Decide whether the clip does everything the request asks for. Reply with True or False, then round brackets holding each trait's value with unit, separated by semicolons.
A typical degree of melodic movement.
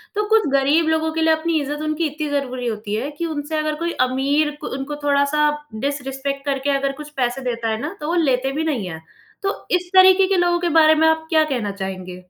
True (3.1 semitones)